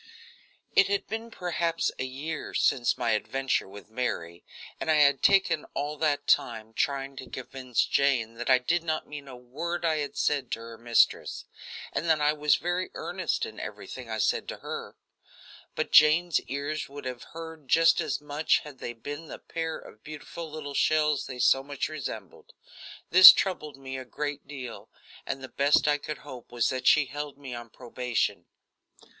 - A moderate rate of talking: Yes, average, 180 wpm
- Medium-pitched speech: Yes, medium, 145 Hz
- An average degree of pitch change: Yes, average, 3.5 semitones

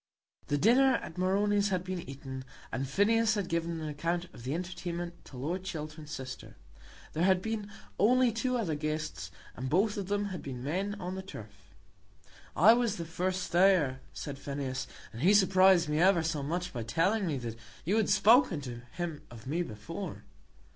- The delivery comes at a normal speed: Yes, average, 180 wpm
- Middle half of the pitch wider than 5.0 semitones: Yes, wide, 5.4 semitones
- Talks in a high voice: No, medium, 175 Hz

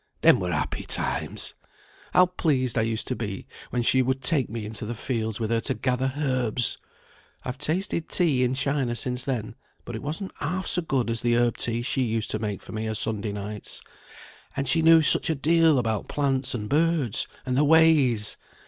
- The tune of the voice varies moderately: Yes, average, 4.6 semitones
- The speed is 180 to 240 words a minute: Yes, average, 200 wpm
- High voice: No, low, 125 Hz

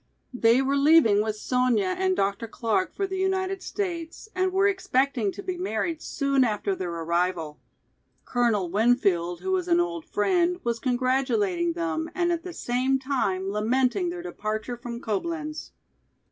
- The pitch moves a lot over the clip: Yes, wide, 8.7 semitones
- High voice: Yes, very high, 255 Hz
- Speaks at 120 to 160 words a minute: Yes, average, 155 wpm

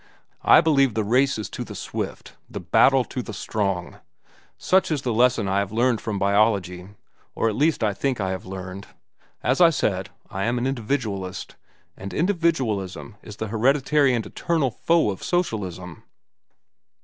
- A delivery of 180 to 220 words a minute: No, average, 160 wpm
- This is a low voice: Yes, low, 110 Hz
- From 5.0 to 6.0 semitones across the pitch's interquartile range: Yes, wide, 5.6 semitones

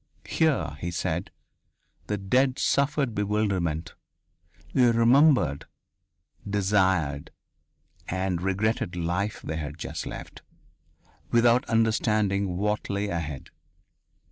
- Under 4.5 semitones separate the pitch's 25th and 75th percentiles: No, average, 4.8 semitones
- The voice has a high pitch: No, low, 100 Hz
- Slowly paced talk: Yes, slow, 95 wpm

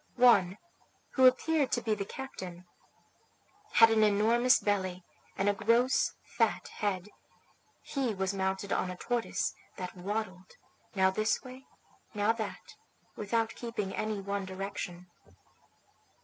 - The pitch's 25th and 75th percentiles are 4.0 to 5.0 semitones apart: No, average, 3.4 semitones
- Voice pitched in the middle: No, high, 205 Hz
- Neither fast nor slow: No, slow, 125 wpm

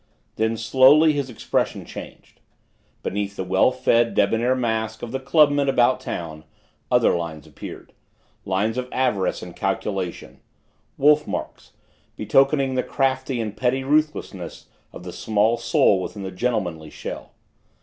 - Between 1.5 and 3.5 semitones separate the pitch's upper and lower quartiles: No, average, 4.9 semitones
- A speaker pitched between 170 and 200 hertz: No, low, 115 Hz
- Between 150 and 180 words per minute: No, slow, 135 wpm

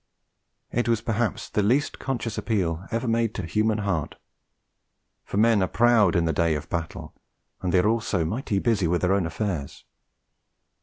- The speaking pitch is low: Yes, low, 105 Hz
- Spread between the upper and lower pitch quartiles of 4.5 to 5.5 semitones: Yes, average, 4.8 semitones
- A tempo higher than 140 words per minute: Yes, average, 170 wpm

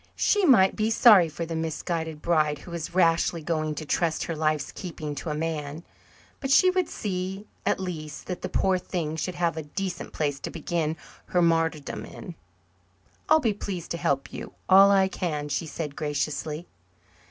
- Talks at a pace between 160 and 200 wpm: Yes, average, 180 wpm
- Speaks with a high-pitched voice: No, medium, 165 Hz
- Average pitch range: Yes, average, 3.4 semitones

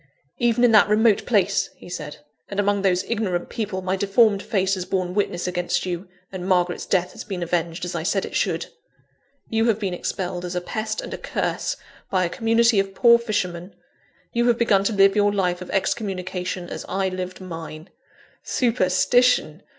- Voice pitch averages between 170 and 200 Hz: Yes, high, 190 Hz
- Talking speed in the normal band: Yes, average, 185 wpm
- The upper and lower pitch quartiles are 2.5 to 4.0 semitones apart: Yes, average, 3.2 semitones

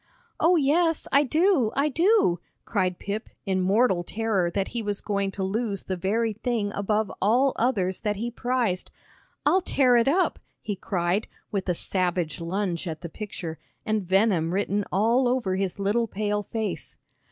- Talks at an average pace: Yes, average, 165 wpm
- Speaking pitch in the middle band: No, high, 205 Hz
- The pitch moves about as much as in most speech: Yes, average, 4.2 semitones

